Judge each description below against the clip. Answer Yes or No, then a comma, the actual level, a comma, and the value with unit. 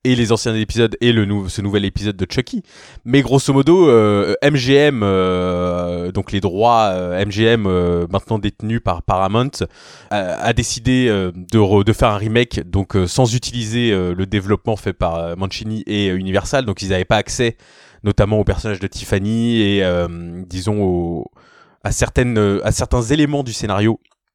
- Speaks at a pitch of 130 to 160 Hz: No, low, 105 Hz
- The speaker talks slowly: No, average, 180 wpm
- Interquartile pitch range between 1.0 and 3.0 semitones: No, average, 3.6 semitones